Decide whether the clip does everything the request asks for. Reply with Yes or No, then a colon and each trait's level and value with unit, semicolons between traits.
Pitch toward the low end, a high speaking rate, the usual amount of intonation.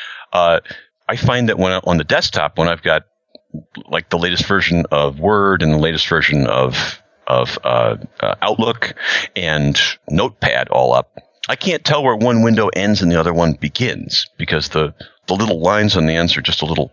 No: very low, 85 Hz; average, 195 wpm; average, 4.0 semitones